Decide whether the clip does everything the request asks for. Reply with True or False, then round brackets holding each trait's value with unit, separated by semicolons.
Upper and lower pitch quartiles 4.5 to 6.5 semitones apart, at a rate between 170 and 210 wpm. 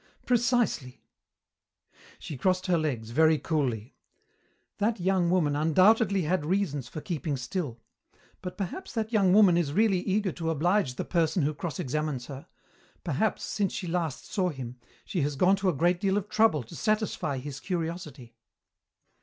False (5.0 semitones; 160 wpm)